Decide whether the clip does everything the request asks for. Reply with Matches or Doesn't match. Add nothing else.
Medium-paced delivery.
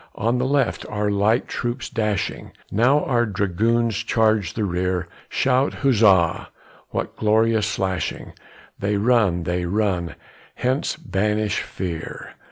Doesn't match